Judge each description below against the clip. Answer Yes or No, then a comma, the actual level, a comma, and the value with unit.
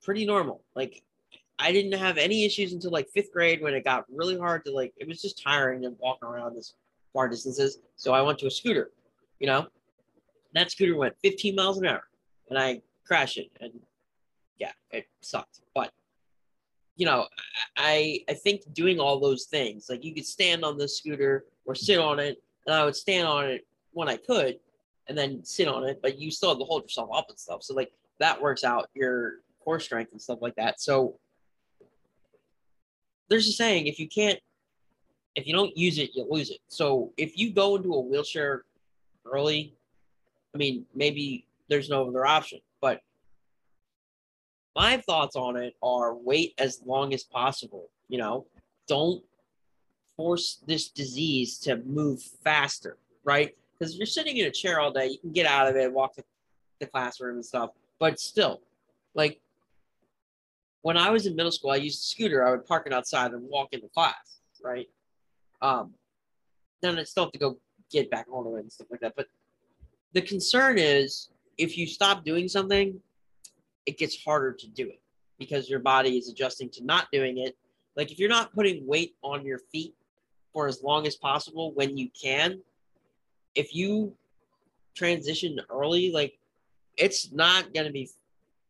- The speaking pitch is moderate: Yes, medium, 145 Hz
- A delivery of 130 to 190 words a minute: Yes, average, 185 wpm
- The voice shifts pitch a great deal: No, average, 4.9 semitones